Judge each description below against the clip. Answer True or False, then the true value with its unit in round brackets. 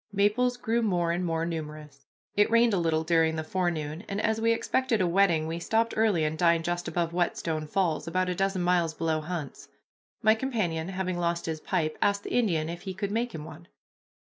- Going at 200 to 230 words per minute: True (205 wpm)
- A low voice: False (175 Hz)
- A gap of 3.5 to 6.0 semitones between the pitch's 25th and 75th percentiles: True (3.9 semitones)